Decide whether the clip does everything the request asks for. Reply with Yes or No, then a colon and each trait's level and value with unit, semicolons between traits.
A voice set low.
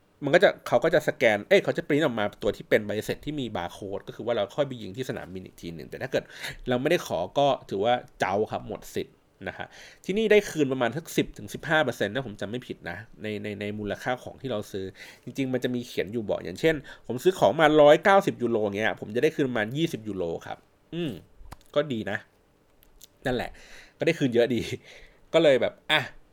Yes: low, 125 Hz